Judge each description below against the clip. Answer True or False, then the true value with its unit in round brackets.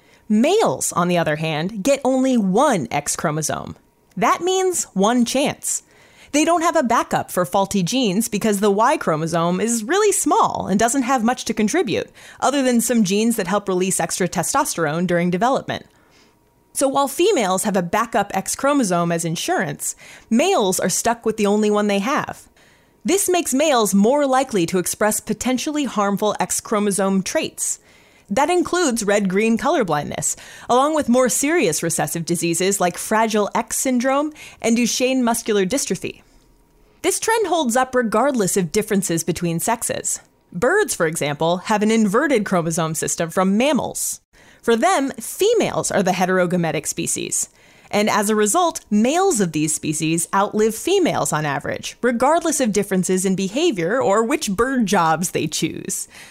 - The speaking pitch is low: False (215 Hz)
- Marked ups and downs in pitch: True (6.1 semitones)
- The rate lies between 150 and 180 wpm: True (155 wpm)